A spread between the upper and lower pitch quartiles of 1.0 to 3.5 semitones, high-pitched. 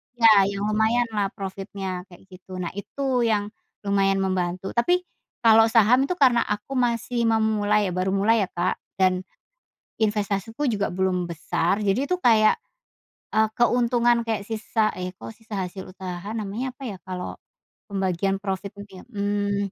Yes: average, 3.0 semitones; high, 205 Hz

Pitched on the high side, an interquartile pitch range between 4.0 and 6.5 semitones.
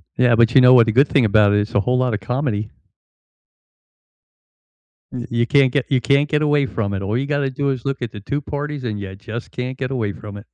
No: low, 125 Hz; average, 4.3 semitones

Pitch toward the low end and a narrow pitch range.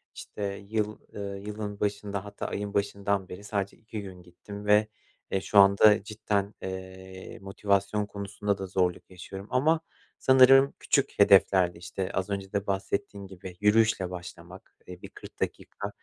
Yes: low, 100 Hz; narrow, 1.6 semitones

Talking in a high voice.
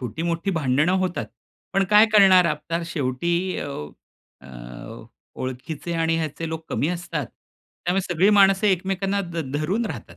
No: medium, 170 Hz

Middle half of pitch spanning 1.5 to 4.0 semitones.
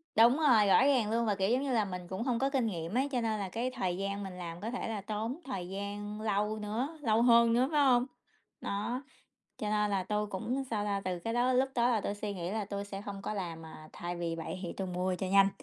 Yes: average, 3.6 semitones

